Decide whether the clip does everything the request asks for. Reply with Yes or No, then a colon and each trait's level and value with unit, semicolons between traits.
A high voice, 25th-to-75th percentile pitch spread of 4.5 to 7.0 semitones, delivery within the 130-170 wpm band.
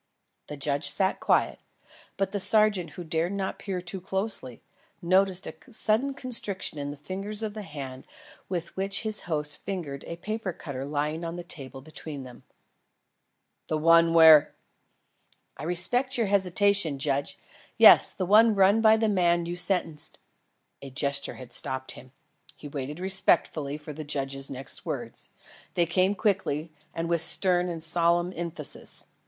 No: medium, 170 Hz; average, 4.8 semitones; average, 160 wpm